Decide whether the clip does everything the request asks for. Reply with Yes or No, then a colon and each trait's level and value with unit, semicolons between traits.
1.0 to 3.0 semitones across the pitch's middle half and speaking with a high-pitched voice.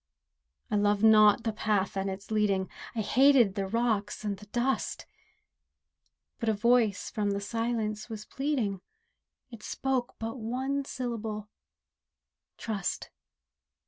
Yes: average, 2.7 semitones; high, 215 Hz